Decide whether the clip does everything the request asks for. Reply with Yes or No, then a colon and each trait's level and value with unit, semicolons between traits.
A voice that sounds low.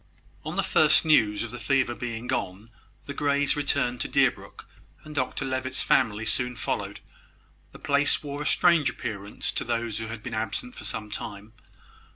Yes: low, 120 Hz